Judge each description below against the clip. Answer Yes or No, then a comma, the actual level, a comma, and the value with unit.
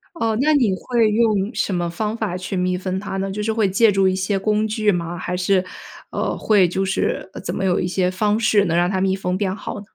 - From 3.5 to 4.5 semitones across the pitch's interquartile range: No, narrow, 2.5 semitones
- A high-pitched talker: Yes, high, 195 Hz